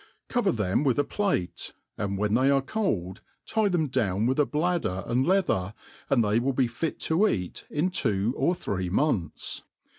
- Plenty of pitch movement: Yes, wide, 8.4 semitones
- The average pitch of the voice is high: No, low, 130 Hz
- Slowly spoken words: No, average, 180 wpm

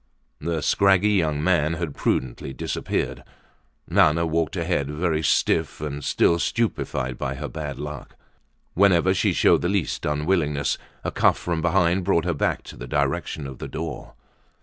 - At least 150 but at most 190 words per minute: Yes, average, 155 wpm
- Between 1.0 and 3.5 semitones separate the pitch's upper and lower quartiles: Yes, average, 3.0 semitones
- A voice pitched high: No, very low, 80 Hz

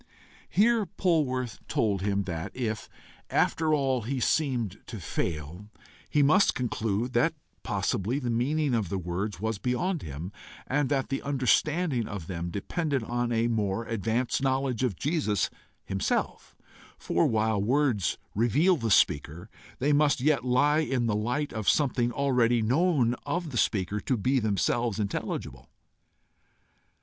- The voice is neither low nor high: No, low, 120 Hz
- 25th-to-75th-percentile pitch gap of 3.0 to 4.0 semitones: No, average, 5.2 semitones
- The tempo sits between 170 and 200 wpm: No, average, 140 wpm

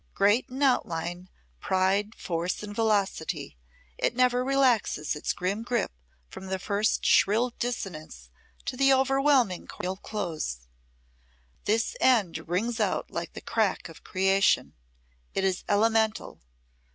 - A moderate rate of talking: No, slow, 125 wpm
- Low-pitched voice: No, high, 205 Hz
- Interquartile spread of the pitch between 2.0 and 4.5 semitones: No, average, 4.9 semitones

